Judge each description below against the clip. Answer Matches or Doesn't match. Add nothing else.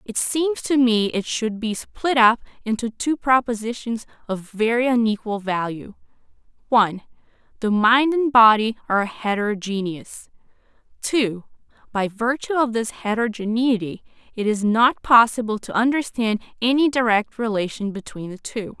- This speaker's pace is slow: Matches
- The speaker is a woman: Matches